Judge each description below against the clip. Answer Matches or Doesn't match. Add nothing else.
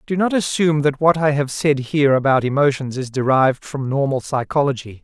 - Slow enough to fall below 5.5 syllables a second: Doesn't match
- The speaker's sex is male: Matches